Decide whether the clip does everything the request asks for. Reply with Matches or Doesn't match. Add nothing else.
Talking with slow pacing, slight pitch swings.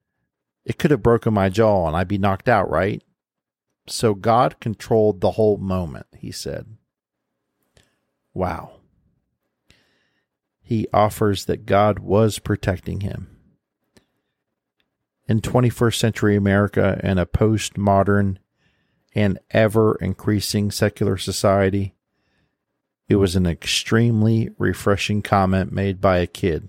Matches